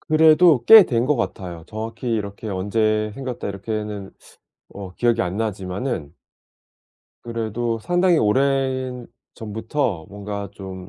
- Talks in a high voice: No, low, 110 Hz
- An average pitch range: Yes, average, 4.1 semitones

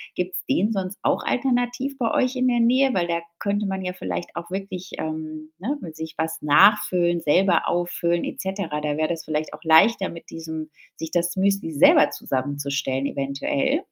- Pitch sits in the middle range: Yes, medium, 175 Hz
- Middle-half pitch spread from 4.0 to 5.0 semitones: Yes, average, 4.3 semitones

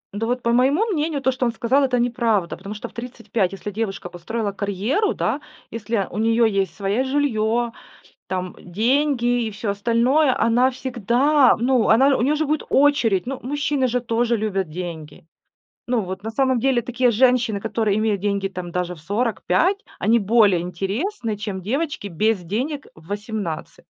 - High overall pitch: Yes, high, 230 Hz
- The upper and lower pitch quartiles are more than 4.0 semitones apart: Yes, average, 4.4 semitones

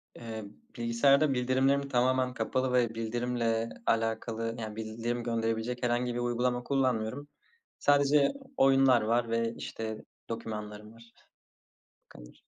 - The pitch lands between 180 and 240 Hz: No, low, 120 Hz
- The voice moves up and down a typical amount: No, narrow, 2.1 semitones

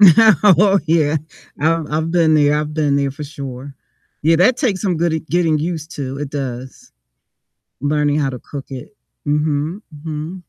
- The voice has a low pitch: No, medium, 155 Hz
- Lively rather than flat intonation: No, average, 2.8 semitones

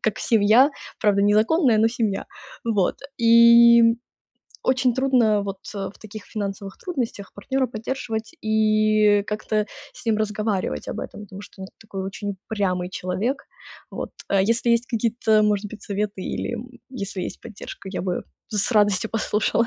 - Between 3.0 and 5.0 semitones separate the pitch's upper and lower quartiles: No, narrow, 2.4 semitones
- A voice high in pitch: Yes, high, 215 Hz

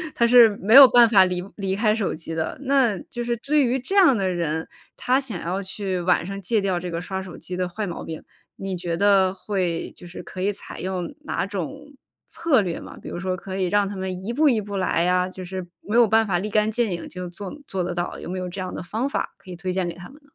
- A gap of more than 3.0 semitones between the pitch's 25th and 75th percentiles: Yes, average, 3.5 semitones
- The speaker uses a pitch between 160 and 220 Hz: Yes, high, 190 Hz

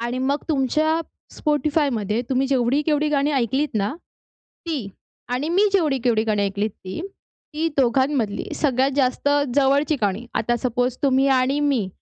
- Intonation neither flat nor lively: Yes, average, 3.6 semitones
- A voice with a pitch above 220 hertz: Yes, very high, 265 Hz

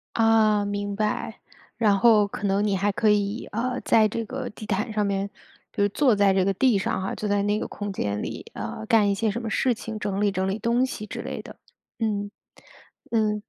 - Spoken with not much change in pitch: Yes, narrow, 1.9 semitones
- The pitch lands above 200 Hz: Yes, high, 210 Hz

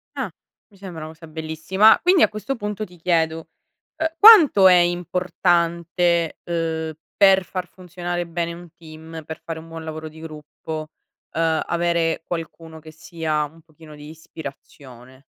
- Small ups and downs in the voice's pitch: Yes, narrow, 1.9 semitones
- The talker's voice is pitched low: No, medium, 165 Hz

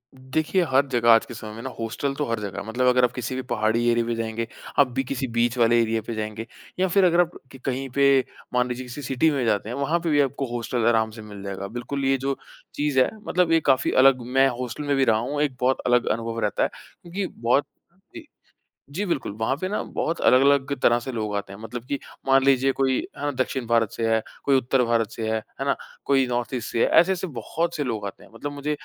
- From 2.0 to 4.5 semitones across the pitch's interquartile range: Yes, average, 3.3 semitones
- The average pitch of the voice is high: No, low, 125 Hz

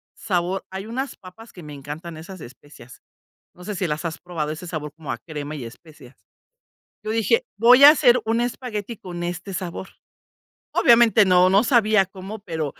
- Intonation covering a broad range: Yes, wide, 5.7 semitones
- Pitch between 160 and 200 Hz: Yes, medium, 185 Hz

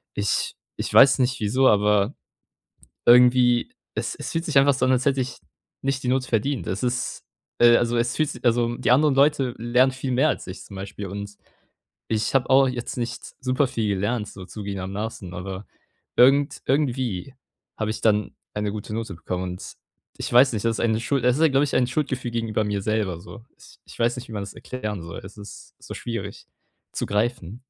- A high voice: No, low, 120 Hz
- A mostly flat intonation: No, average, 3.8 semitones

